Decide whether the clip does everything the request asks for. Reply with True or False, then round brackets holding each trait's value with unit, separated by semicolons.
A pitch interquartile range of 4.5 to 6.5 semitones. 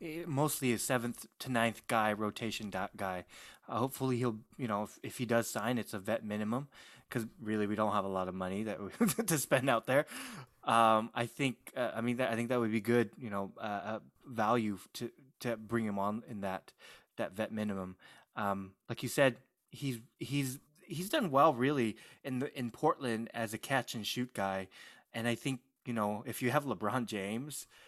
False (3.4 semitones)